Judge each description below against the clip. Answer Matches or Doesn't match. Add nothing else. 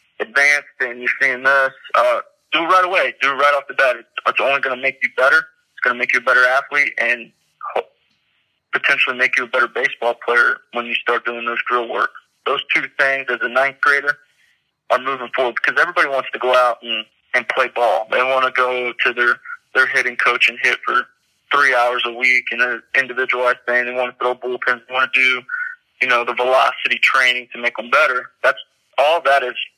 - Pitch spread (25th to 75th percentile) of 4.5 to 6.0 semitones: Doesn't match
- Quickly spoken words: Matches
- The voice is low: Matches